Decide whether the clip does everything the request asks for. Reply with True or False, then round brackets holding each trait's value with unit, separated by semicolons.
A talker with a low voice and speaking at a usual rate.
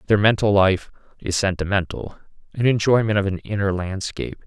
True (100 Hz; 150 wpm)